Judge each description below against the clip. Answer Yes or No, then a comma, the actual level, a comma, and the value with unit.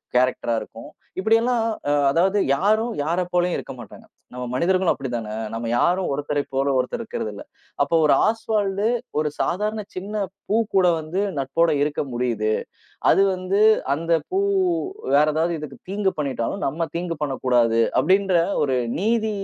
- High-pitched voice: No, medium, 170 Hz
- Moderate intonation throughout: No, wide, 6.6 semitones